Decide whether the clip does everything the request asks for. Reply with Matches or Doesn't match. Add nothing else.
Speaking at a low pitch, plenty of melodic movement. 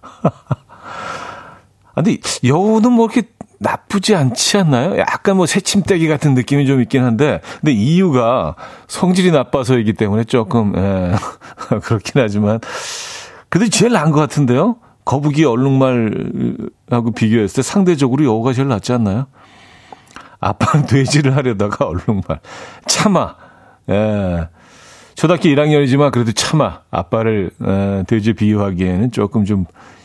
Matches